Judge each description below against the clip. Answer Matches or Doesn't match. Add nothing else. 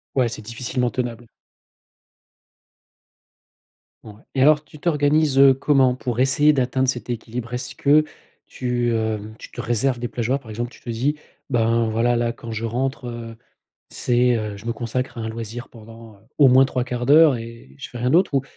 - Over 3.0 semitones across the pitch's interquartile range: Doesn't match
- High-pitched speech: Doesn't match